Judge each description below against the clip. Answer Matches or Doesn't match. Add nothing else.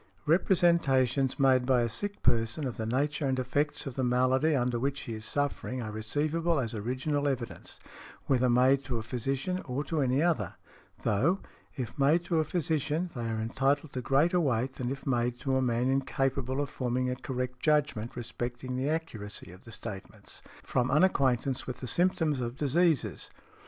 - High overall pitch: Doesn't match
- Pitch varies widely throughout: Doesn't match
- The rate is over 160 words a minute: Matches